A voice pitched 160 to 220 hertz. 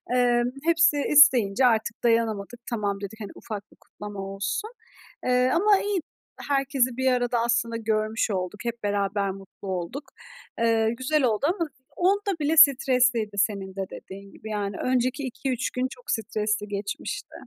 No: high, 235 Hz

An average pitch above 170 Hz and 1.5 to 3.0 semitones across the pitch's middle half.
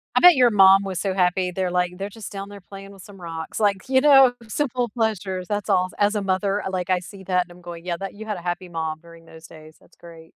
Yes: high, 190 Hz; average, 2.7 semitones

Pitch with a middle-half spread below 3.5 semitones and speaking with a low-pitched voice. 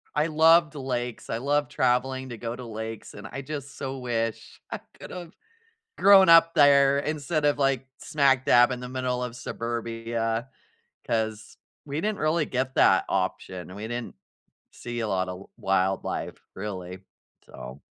No: average, 4.0 semitones; low, 125 Hz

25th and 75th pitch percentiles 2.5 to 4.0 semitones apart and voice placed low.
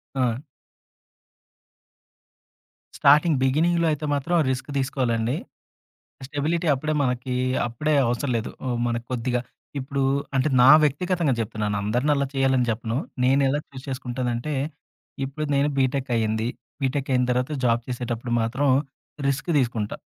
Yes: average, 2.9 semitones; low, 130 Hz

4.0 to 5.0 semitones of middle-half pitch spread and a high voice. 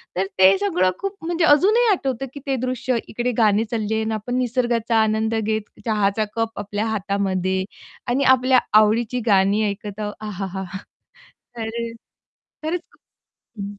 No: average, 3.6 semitones; high, 220 Hz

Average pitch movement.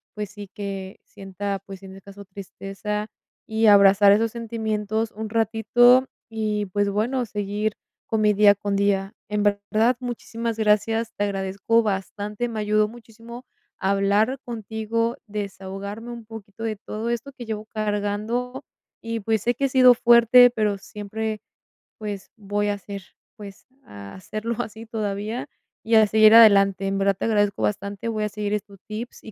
No: narrow, 2.1 semitones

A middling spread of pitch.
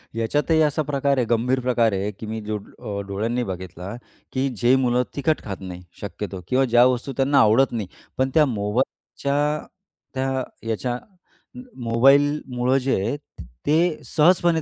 Yes: average, 4.1 semitones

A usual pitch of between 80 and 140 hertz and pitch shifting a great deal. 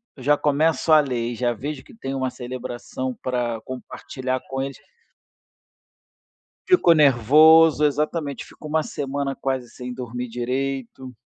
No: low, 135 Hz; average, 2.9 semitones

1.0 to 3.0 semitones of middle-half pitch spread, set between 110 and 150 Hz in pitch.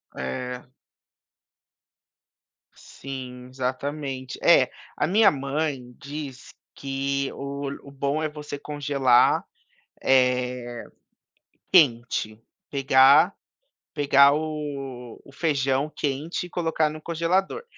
Yes: average, 2.7 semitones; medium, 140 Hz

